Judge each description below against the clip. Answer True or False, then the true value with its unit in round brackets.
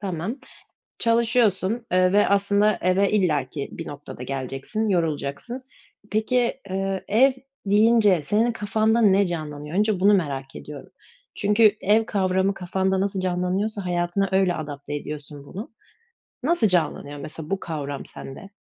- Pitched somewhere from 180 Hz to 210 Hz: True (190 Hz)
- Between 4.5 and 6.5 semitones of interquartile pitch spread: True (5.2 semitones)